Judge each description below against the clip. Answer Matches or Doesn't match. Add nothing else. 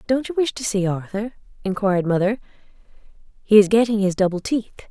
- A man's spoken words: Doesn't match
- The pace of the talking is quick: Doesn't match